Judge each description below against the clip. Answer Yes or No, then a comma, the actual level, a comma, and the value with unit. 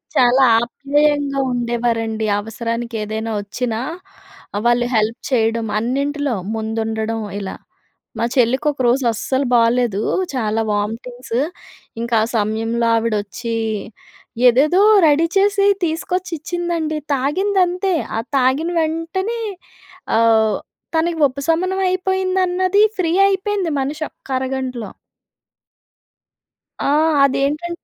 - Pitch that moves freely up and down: Yes, wide, 6.3 semitones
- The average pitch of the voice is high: Yes, very high, 260 Hz